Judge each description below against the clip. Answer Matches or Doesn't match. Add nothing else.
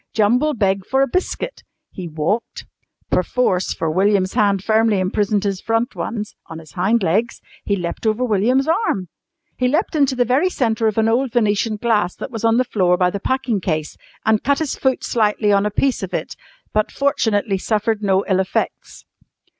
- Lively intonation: Doesn't match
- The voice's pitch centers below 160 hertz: Doesn't match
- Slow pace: Doesn't match